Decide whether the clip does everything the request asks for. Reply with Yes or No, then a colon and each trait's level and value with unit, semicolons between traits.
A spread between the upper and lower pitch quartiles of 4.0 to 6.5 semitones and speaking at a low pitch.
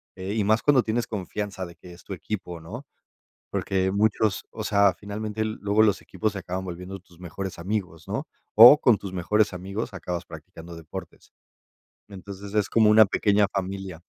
No: average, 2.7 semitones; low, 100 Hz